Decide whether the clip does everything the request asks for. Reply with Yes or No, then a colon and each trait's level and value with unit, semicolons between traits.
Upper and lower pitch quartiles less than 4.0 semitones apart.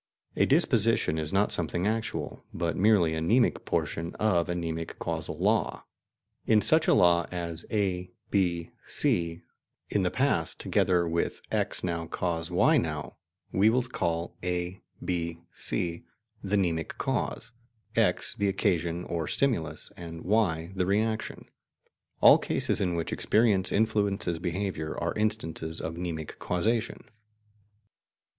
Yes: average, 3.4 semitones